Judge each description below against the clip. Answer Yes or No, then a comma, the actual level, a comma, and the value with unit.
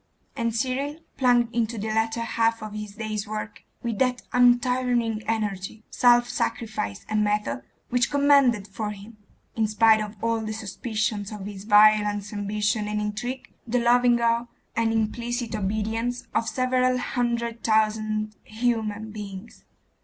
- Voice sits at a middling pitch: No, high, 220 Hz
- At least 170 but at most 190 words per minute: No, average, 140 wpm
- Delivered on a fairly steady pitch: Yes, narrow, 2.2 semitones